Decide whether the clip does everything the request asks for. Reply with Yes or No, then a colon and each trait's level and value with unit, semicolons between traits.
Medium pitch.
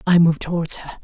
Yes: medium, 170 Hz